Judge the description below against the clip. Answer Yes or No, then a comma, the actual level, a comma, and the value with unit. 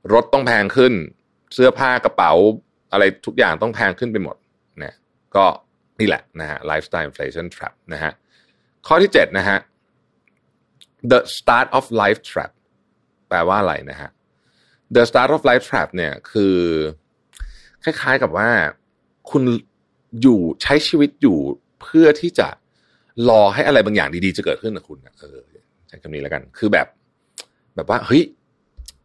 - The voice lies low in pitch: Yes, low, 105 Hz